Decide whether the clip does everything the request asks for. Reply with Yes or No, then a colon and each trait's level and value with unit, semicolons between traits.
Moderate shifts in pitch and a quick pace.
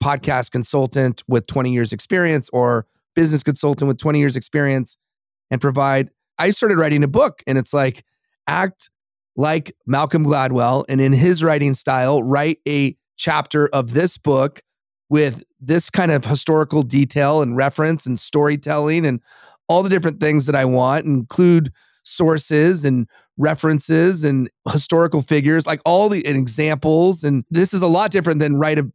No: average, 3.0 semitones; average, 160 wpm